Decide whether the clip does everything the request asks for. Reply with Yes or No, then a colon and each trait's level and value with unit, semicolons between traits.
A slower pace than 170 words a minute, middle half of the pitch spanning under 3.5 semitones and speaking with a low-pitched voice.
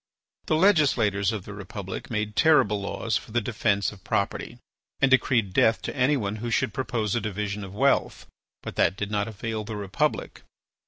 No: average, 175 wpm; average, 2.9 semitones; low, 105 Hz